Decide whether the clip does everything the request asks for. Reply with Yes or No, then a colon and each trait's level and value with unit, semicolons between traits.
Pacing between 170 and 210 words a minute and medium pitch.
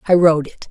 No: fast, 255 wpm; medium, 165 Hz